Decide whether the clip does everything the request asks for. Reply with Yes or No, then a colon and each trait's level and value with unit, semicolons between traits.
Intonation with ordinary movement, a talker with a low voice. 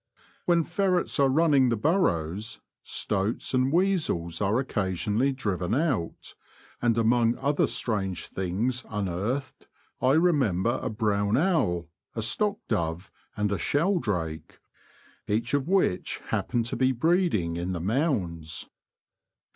No: wide, 7.0 semitones; low, 115 Hz